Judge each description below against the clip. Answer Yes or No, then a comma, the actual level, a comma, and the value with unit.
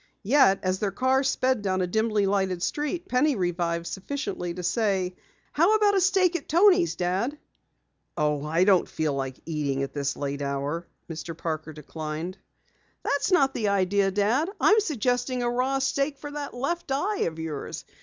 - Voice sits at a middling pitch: No, high, 200 Hz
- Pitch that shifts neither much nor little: No, wide, 8.8 semitones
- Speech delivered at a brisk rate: No, average, 170 wpm